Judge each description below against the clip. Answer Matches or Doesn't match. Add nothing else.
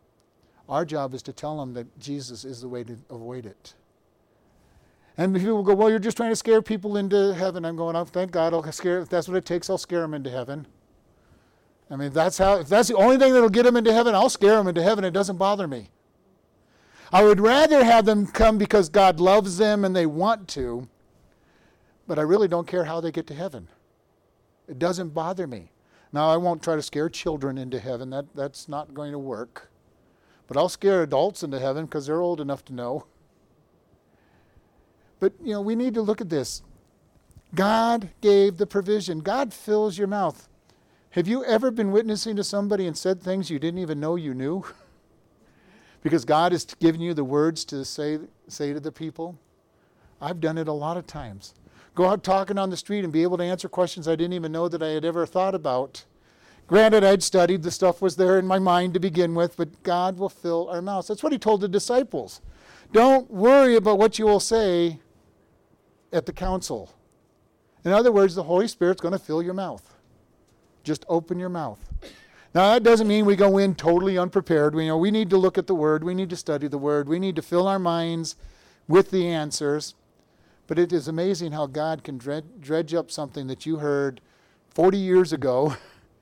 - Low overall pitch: Doesn't match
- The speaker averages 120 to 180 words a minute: Doesn't match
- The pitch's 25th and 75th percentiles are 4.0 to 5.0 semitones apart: Matches